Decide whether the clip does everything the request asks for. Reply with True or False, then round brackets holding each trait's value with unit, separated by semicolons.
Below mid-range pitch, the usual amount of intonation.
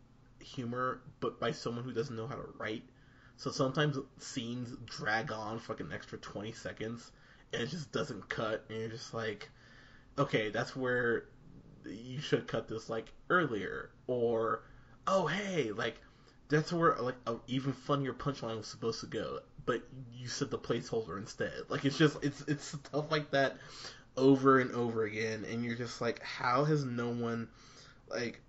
True (125 Hz; 3.2 semitones)